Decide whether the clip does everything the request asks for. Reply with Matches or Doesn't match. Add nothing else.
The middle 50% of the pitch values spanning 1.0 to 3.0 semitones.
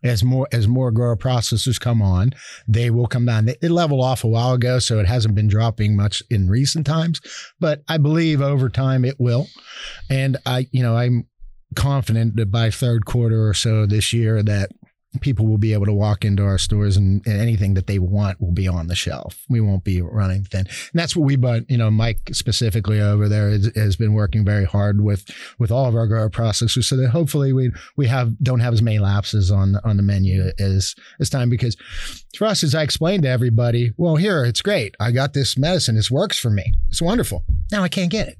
Doesn't match